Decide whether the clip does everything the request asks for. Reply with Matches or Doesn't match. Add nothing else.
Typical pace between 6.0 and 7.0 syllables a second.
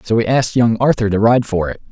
Matches